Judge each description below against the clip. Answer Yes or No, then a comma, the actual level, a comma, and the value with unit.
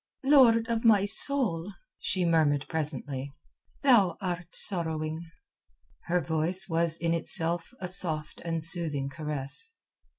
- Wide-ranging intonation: No, average, 3.6 semitones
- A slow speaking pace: Yes, slow, 120 wpm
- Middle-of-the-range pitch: Yes, medium, 170 Hz